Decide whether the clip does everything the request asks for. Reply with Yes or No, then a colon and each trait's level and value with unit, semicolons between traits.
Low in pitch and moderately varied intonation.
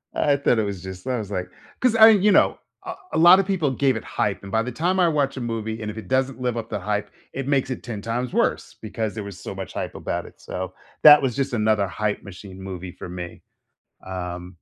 No: low, 110 Hz; wide, 5.8 semitones